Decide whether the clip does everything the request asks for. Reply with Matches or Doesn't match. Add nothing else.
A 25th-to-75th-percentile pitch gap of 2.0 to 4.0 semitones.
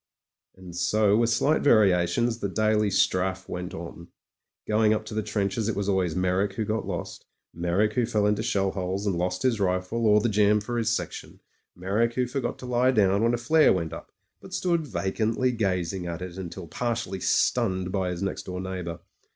Matches